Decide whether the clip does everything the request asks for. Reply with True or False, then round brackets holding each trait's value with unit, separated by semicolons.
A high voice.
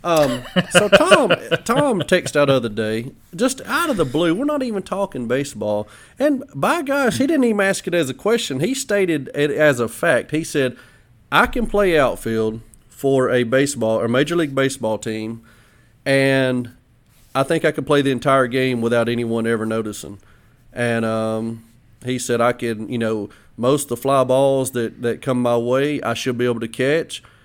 False (130 Hz)